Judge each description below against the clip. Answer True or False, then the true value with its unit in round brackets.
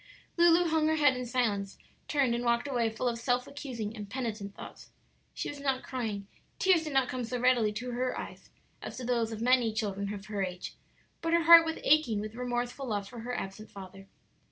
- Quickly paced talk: True (210 wpm)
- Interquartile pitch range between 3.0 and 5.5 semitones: True (3.9 semitones)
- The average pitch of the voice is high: True (245 Hz)